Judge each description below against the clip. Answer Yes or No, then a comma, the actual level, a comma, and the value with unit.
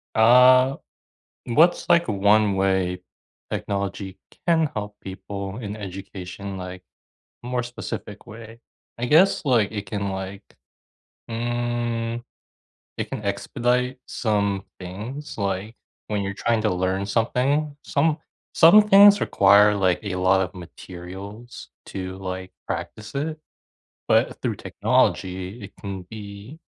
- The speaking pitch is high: No, low, 105 Hz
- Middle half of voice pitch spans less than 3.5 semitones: No, average, 4.0 semitones